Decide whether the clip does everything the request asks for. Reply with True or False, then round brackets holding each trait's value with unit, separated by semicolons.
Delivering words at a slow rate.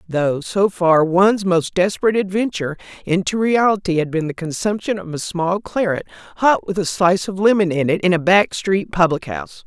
False (190 wpm)